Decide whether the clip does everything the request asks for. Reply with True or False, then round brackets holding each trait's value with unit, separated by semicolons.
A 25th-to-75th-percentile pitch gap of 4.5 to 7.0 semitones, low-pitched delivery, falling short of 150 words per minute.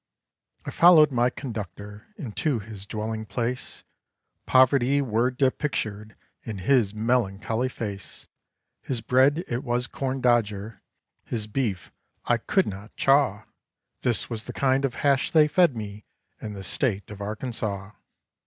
False (3.9 semitones; 120 Hz; 135 wpm)